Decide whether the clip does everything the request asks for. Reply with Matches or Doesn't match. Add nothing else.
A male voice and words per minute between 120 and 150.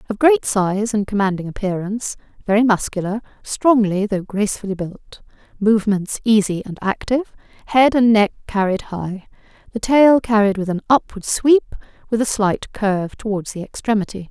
Doesn't match